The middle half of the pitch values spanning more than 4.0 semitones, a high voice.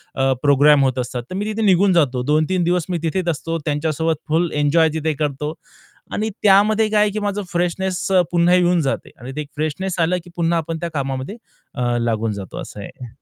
No: average, 4.4 semitones; medium, 165 Hz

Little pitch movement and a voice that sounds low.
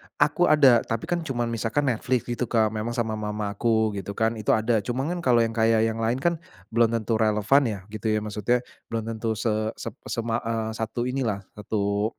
Yes: narrow, 1.9 semitones; low, 115 Hz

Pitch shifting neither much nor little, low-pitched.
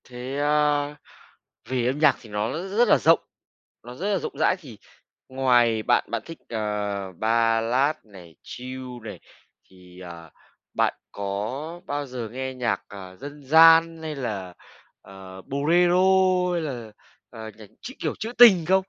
No: wide, 7.0 semitones; low, 130 Hz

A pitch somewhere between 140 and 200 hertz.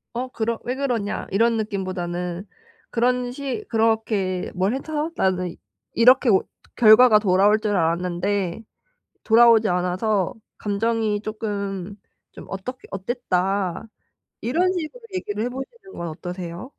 No: high, 215 Hz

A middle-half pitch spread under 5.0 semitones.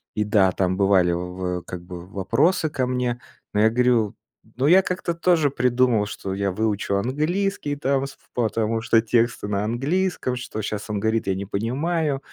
No: wide, 5.4 semitones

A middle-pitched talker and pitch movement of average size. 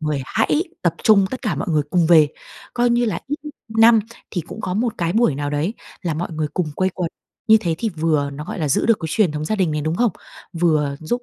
No: medium, 175 Hz; wide, 6.2 semitones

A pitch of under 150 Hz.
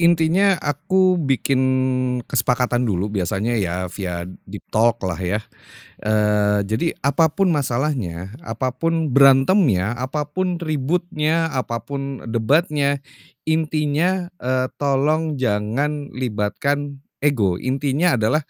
Yes: low, 135 Hz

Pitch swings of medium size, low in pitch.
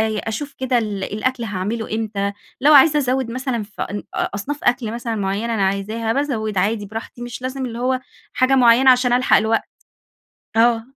No: average, 3.2 semitones; high, 230 Hz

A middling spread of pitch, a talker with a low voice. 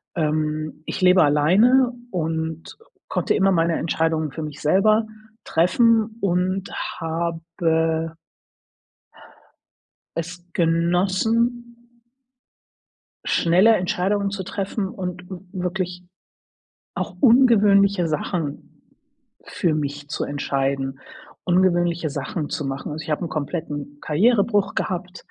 No: average, 3.8 semitones; medium, 175 Hz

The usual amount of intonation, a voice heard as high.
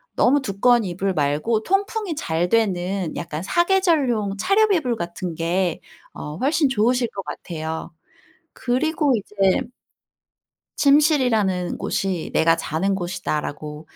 No: wide, 7.4 semitones; high, 200 Hz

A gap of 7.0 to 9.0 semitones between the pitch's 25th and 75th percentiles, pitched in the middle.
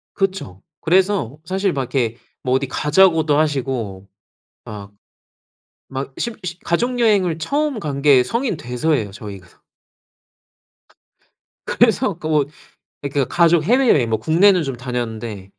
Yes: wide, 7.5 semitones; medium, 150 Hz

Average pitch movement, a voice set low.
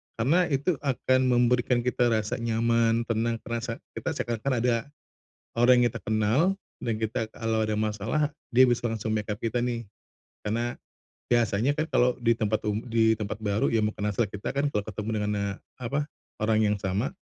No: narrow, 2.2 semitones; low, 115 Hz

